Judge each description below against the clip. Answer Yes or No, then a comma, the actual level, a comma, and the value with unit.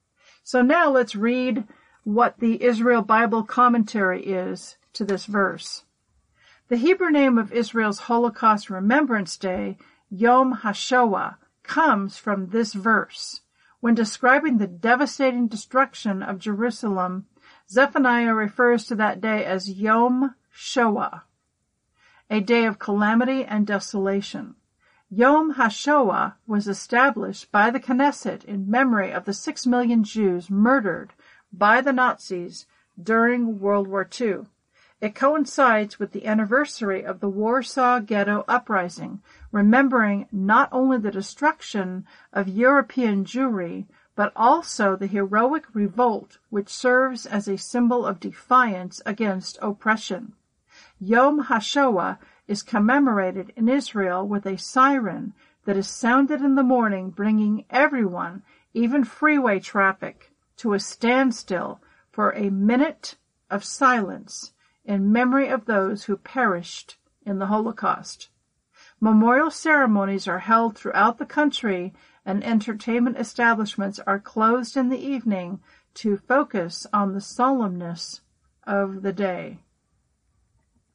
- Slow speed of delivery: Yes, slow, 120 wpm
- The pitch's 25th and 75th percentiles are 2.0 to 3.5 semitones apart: No, average, 4.2 semitones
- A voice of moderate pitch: No, high, 225 Hz